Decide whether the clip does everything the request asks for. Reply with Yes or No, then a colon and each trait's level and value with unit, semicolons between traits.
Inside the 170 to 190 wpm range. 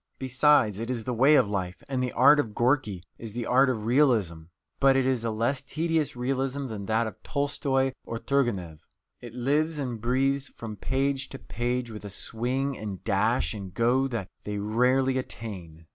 Yes: average, 185 wpm